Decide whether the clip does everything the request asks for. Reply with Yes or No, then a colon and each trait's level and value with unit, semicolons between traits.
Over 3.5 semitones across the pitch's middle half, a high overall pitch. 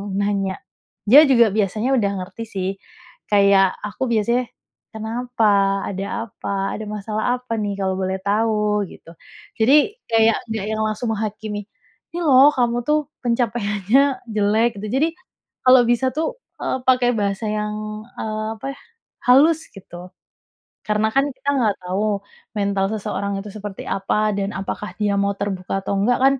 No: average, 3.1 semitones; high, 215 Hz